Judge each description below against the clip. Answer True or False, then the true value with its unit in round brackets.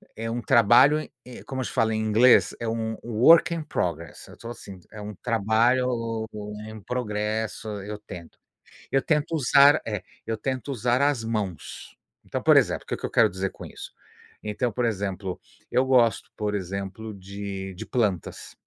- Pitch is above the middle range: False (110 Hz)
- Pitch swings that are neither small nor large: True (3.4 semitones)